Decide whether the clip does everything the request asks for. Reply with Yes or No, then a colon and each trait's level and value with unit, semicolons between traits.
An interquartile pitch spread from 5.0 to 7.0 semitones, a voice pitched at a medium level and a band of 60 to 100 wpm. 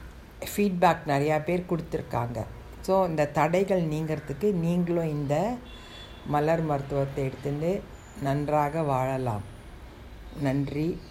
No: average, 3.8 semitones; medium, 150 Hz; average, 85 wpm